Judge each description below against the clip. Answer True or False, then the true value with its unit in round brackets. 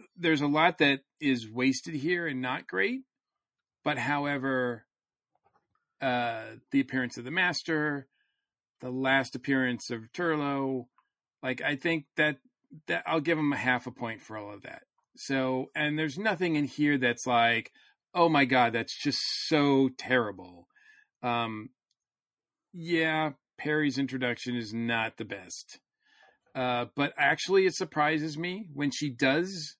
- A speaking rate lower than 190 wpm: True (145 wpm)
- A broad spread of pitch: False (4.1 semitones)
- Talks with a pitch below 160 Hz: True (140 Hz)